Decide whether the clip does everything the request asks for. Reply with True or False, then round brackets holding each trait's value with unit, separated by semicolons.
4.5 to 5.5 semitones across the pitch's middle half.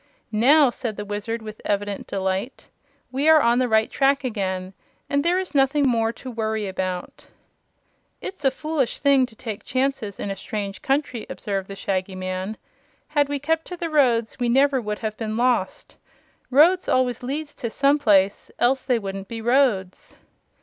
True (5.1 semitones)